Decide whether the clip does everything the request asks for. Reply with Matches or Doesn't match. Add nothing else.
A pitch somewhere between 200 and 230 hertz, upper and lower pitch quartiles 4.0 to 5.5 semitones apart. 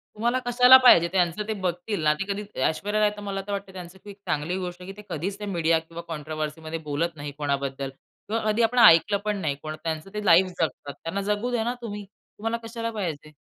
Doesn't match